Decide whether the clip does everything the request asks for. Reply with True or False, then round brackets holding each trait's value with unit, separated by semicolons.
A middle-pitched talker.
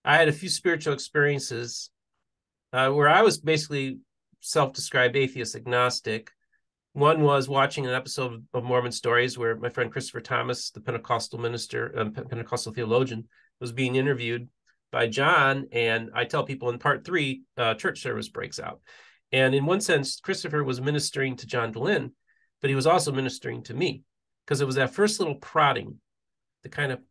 False (130 Hz)